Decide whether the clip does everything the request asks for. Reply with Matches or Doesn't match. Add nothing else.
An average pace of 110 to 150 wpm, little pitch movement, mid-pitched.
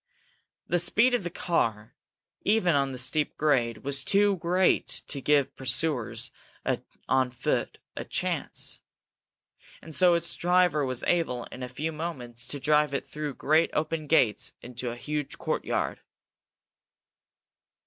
Doesn't match